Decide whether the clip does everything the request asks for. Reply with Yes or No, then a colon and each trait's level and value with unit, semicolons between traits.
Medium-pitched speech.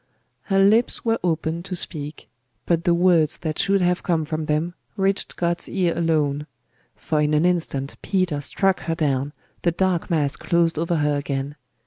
Yes: medium, 165 Hz